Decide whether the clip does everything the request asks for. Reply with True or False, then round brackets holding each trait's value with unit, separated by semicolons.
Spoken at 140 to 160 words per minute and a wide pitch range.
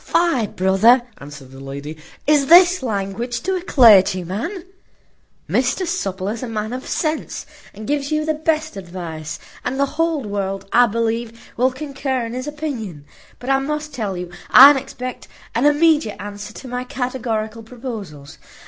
True (155 wpm; 6.2 semitones)